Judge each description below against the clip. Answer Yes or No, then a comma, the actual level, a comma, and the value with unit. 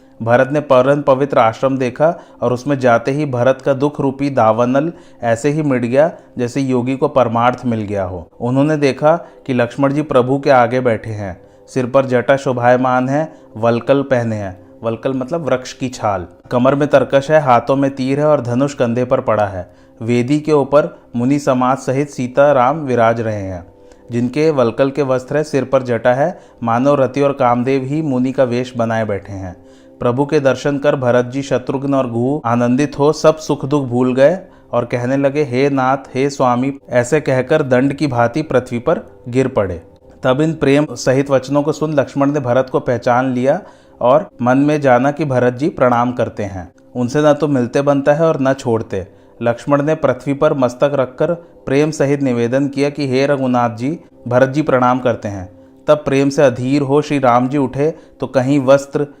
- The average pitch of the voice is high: No, low, 130 Hz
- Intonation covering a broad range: No, average, 2.8 semitones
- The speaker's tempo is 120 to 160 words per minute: No, fast, 190 wpm